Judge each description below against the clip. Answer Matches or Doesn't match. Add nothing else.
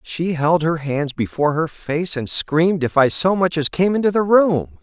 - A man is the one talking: Matches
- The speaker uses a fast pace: Matches